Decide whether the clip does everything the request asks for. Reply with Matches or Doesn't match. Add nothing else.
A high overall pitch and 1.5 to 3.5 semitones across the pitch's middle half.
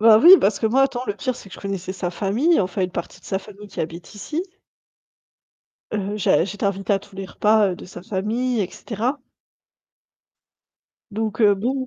Matches